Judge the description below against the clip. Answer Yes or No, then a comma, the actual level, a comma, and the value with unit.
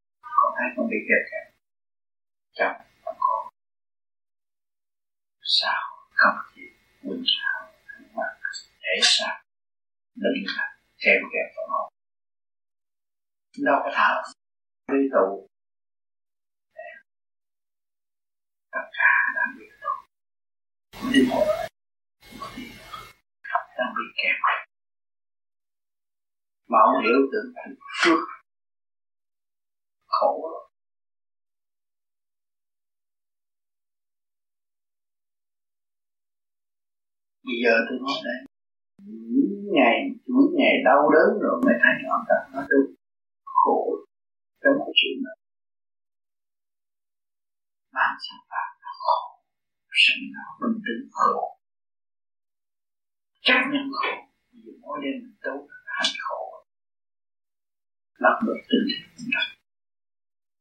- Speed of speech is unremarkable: No, slow, 70 wpm